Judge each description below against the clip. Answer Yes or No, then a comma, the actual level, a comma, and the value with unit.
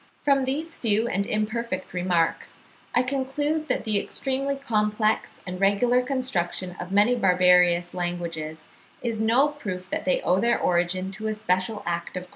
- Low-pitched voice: No, high, 210 Hz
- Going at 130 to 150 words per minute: No, average, 160 wpm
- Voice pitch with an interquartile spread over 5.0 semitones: Yes, wide, 5.5 semitones